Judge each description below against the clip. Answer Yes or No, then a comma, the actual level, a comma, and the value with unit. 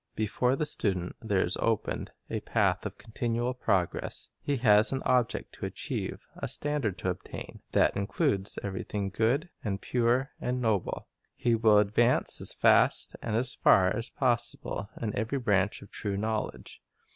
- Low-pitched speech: Yes, low, 110 Hz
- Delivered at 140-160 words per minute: Yes, average, 155 wpm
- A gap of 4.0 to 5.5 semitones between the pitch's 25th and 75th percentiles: No, average, 3.5 semitones